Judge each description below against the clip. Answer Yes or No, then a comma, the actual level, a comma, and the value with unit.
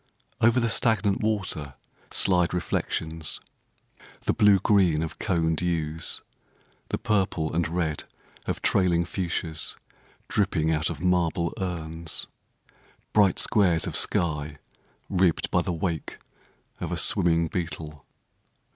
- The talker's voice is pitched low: Yes, very low, 85 Hz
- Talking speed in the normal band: No, slow, 115 wpm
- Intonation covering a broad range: No, average, 2.9 semitones